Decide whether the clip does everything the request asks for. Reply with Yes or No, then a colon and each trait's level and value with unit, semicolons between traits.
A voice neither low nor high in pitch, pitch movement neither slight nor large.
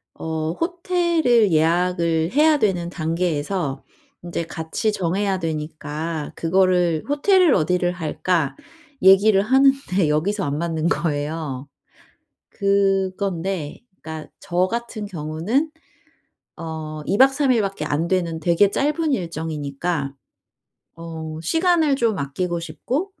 Yes: medium, 175 Hz; average, 4.8 semitones